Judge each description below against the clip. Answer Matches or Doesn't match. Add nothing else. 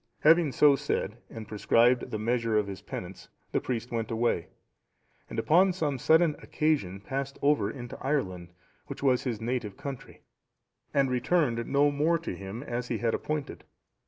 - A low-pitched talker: Matches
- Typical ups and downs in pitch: Matches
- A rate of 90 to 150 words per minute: Doesn't match